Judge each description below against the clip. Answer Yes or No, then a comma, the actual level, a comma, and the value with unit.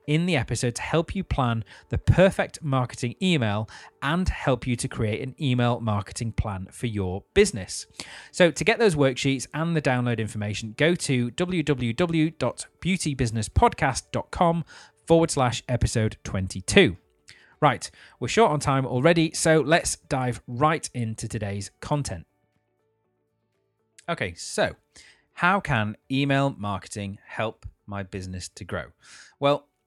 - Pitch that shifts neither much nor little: No, wide, 6.1 semitones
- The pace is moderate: No, slow, 130 wpm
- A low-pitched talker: Yes, low, 125 Hz